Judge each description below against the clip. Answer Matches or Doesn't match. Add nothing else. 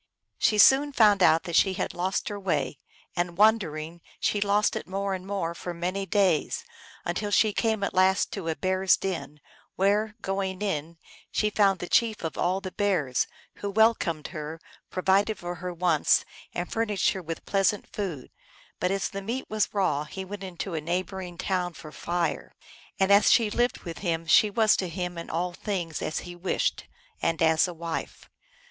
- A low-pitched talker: Doesn't match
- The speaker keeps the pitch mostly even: Doesn't match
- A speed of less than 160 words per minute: Doesn't match